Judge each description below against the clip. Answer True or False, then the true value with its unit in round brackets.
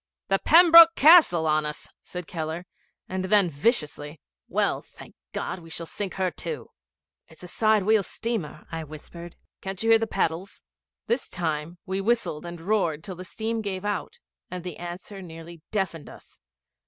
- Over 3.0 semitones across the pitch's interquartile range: True (4.7 semitones)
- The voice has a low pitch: False (185 Hz)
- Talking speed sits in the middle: True (165 wpm)